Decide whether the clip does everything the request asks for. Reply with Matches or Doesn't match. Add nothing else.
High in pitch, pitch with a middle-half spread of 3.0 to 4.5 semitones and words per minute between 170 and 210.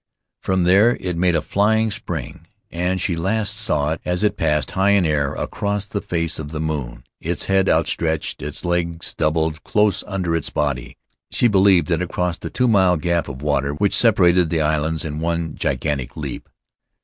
Doesn't match